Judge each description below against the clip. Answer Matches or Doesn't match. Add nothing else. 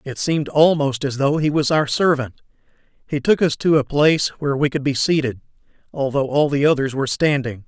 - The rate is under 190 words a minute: Doesn't match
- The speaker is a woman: Doesn't match